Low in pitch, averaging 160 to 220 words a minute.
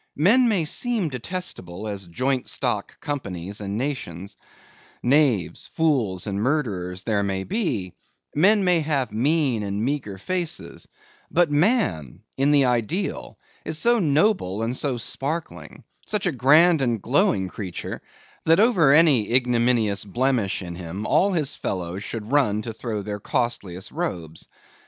No: low, 125 Hz; average, 140 wpm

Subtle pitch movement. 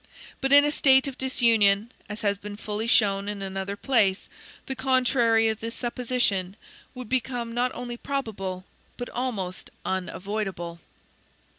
No: average, 4.1 semitones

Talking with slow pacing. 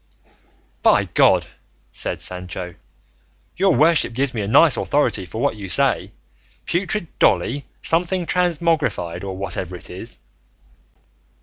Yes: slow, 120 wpm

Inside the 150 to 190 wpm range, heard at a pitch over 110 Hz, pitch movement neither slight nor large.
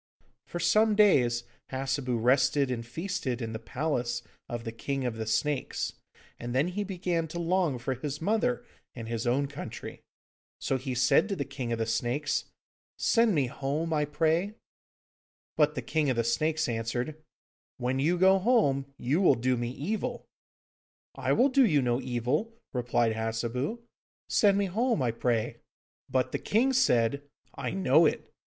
No: average, 165 wpm; medium, 140 Hz; wide, 6.5 semitones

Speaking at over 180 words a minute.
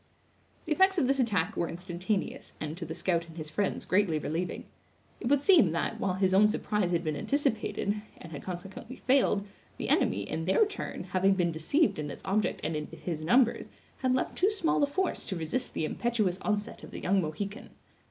Yes: average, 200 wpm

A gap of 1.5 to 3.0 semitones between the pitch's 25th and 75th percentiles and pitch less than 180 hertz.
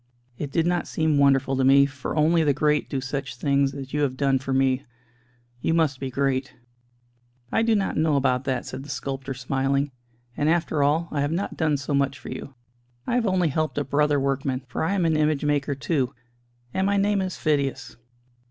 Yes: narrow, 2.6 semitones; medium, 140 Hz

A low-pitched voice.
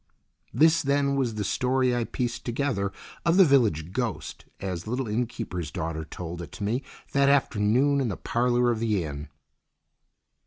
Yes: low, 120 Hz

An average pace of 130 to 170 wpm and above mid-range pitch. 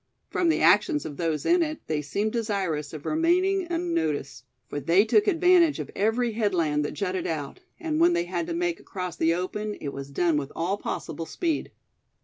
No: average, 190 wpm; high, 210 Hz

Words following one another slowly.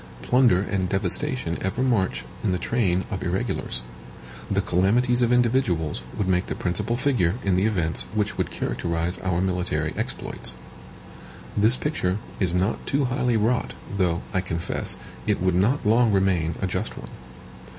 No: average, 155 wpm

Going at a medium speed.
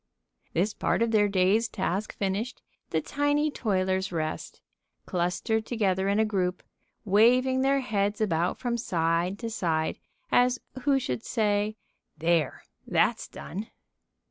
No: slow, 130 wpm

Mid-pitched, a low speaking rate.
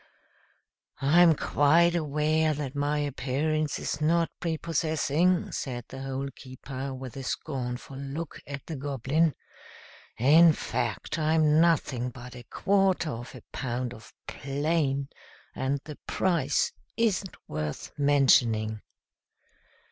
Yes: medium, 145 Hz; slow, 115 wpm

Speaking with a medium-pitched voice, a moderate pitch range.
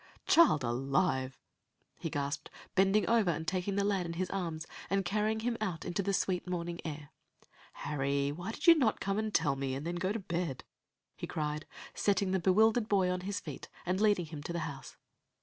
Yes: medium, 180 Hz; average, 4.7 semitones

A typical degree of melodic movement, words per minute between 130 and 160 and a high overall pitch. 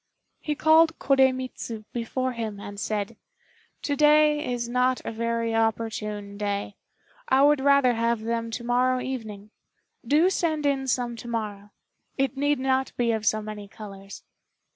Yes: average, 3.7 semitones; average, 150 wpm; high, 240 Hz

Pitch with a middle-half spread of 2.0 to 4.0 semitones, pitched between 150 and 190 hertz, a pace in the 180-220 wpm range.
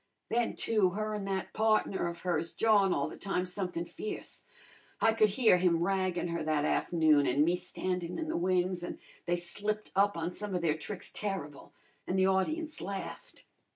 Yes: average, 3.3 semitones; medium, 185 Hz; average, 185 wpm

